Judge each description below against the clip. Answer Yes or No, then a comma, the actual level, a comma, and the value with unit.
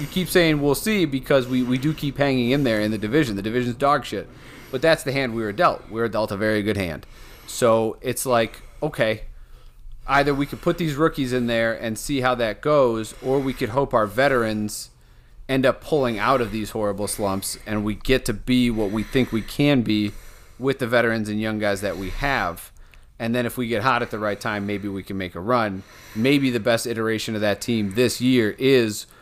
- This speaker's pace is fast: Yes, fast, 230 wpm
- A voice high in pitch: No, low, 115 Hz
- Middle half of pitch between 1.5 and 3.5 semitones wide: No, average, 3.9 semitones